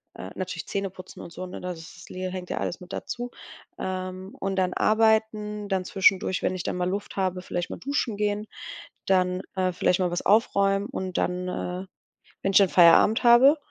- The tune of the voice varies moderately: No, narrow, 2.2 semitones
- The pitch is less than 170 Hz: No, high, 190 Hz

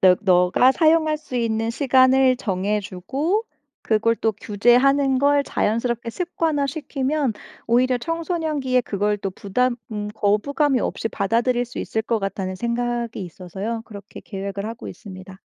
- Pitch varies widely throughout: No, average, 4.8 semitones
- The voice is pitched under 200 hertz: No, high, 235 Hz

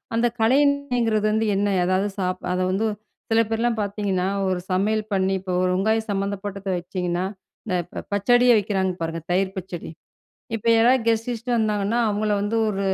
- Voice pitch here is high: Yes, high, 205 Hz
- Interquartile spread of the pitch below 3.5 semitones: Yes, average, 3.1 semitones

